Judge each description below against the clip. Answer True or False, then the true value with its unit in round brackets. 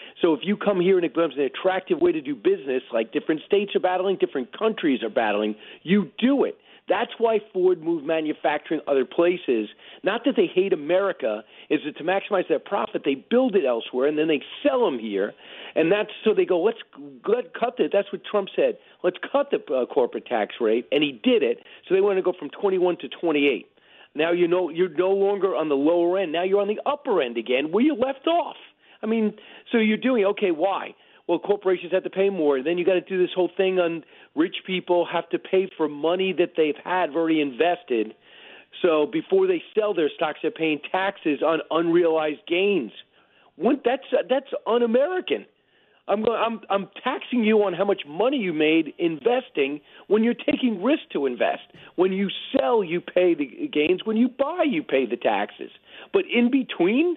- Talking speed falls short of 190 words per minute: False (200 wpm)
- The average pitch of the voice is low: False (195 Hz)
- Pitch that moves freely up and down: True (7.4 semitones)